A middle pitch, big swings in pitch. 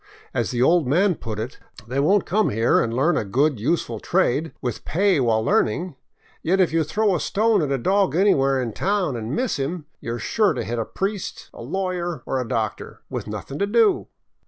Yes: medium, 155 Hz; wide, 7.9 semitones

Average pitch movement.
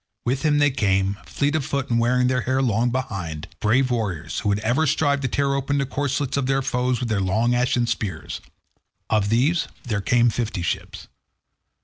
Yes: average, 3.9 semitones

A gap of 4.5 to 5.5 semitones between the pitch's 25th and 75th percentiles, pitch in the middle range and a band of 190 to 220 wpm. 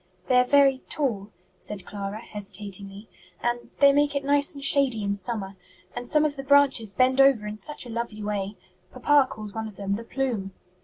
No: average, 5.1 semitones; high, 235 Hz; average, 195 wpm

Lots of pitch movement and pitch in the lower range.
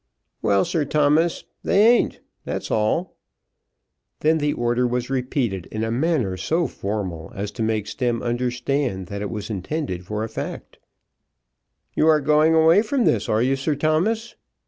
Yes: wide, 6.6 semitones; low, 125 Hz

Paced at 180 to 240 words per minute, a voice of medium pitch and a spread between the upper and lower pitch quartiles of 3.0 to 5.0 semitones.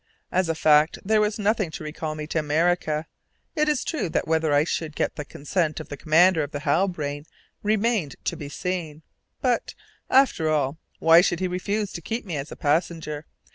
Yes: average, 195 wpm; medium, 160 Hz; average, 3.8 semitones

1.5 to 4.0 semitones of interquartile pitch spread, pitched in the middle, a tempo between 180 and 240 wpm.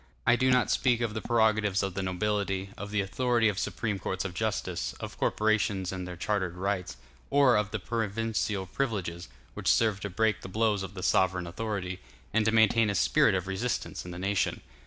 No: average, 2.9 semitones; low, 100 Hz; average, 195 wpm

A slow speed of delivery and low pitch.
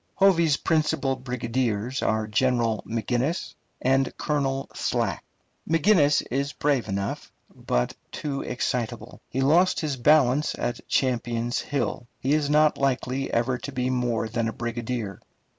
Yes: slow, 130 wpm; low, 130 Hz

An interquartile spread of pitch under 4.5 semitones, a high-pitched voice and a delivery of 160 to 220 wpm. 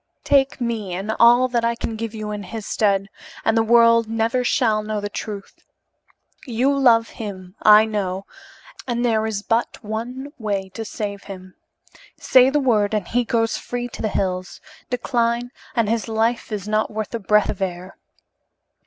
Yes: narrow, 2.4 semitones; high, 220 Hz; average, 175 wpm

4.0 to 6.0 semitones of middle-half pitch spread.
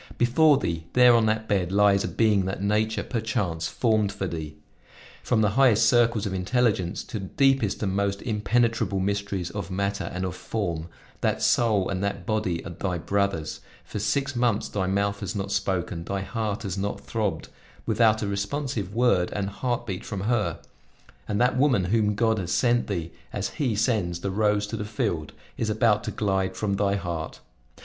No: average, 2.8 semitones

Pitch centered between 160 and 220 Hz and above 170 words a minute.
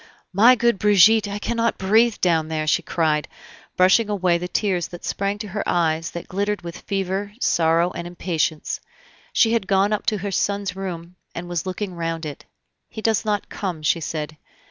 Yes: medium, 185 Hz; average, 185 wpm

